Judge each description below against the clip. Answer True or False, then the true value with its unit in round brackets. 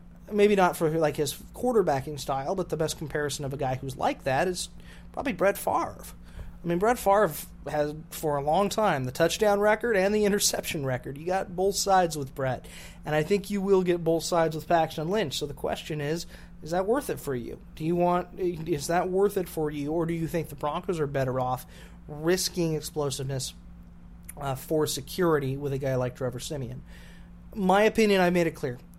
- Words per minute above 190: True (205 wpm)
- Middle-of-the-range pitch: True (160 Hz)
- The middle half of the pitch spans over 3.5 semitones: True (4.7 semitones)